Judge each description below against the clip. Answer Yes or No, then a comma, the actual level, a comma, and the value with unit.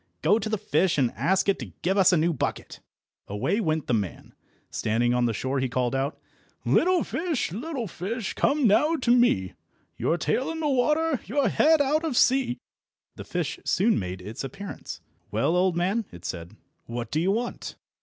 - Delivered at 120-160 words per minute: No, average, 190 wpm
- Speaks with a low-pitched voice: No, high, 190 Hz